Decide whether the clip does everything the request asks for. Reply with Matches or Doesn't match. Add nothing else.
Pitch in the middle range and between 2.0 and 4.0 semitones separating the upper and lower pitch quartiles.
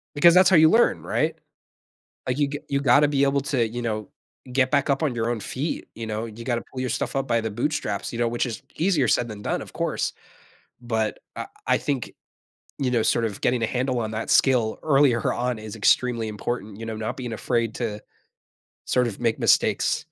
Doesn't match